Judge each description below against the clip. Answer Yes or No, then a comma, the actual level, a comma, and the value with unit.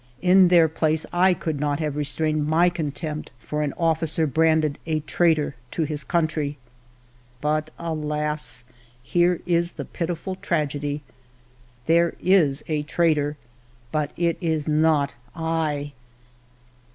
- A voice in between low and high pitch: Yes, medium, 155 Hz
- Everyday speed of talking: No, slow, 125 wpm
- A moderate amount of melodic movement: No, narrow, 2.1 semitones